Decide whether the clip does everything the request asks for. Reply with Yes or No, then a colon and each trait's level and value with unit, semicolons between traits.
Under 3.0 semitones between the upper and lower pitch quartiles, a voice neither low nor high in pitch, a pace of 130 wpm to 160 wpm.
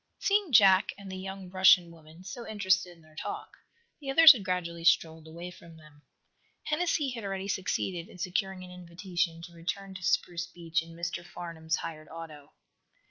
No: narrow, 2.5 semitones; medium, 180 Hz; average, 175 wpm